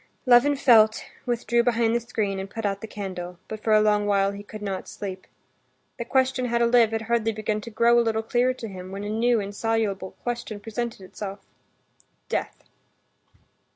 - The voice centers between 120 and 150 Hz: No, high, 220 Hz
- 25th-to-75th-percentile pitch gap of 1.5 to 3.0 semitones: Yes, average, 2.7 semitones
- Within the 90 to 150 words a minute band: No, average, 185 wpm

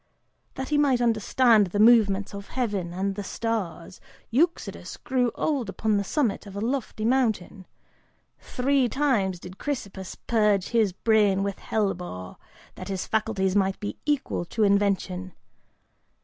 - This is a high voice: Yes, high, 210 Hz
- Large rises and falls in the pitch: No, average, 3.9 semitones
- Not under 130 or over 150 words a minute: Yes, average, 140 wpm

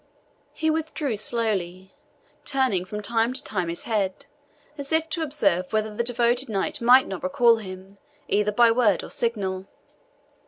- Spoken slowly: No, average, 155 wpm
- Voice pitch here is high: Yes, high, 225 Hz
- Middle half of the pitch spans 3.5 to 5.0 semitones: Yes, average, 4.5 semitones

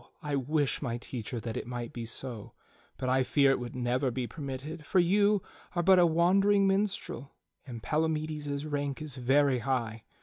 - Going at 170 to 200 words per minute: Yes, average, 175 wpm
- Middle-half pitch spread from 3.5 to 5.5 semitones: Yes, average, 4.3 semitones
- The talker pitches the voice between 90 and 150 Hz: Yes, medium, 140 Hz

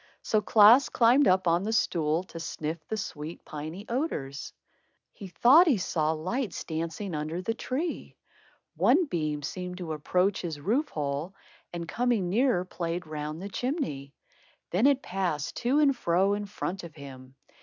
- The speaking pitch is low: No, medium, 180 Hz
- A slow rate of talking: No, average, 160 wpm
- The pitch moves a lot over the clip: Yes, wide, 6.3 semitones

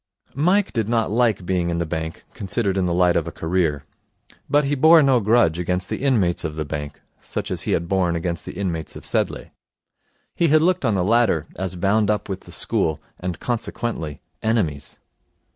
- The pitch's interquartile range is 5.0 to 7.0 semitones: Yes, wide, 5.6 semitones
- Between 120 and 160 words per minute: No, average, 195 wpm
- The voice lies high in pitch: No, very low, 95 Hz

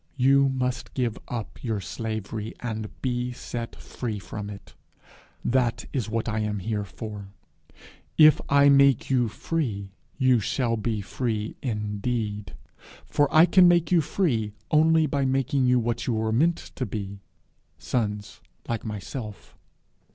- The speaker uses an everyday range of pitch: Yes, average, 4.0 semitones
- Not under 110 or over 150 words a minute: Yes, average, 145 wpm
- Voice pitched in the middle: No, low, 120 Hz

